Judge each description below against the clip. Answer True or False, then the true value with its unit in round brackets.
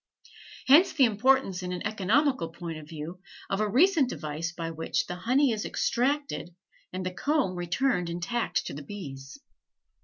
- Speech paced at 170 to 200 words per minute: False (160 wpm)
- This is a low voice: False (185 Hz)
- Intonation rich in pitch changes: True (7.4 semitones)